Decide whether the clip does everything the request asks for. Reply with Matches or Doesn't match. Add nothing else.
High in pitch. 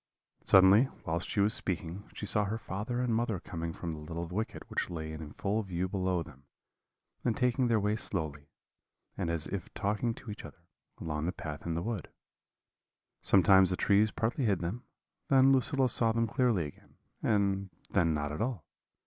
Doesn't match